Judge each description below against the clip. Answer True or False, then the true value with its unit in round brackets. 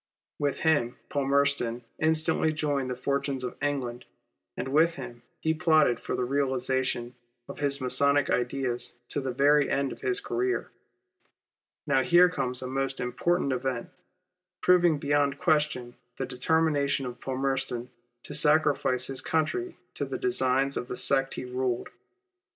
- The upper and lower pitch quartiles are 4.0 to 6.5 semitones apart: False (3.1 semitones)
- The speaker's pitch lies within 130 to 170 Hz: True (140 Hz)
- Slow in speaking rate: False (145 wpm)